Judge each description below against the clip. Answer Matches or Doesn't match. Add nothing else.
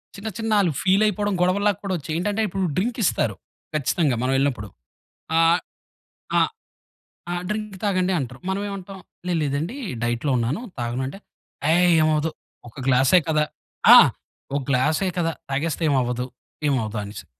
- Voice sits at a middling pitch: Matches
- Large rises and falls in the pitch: Matches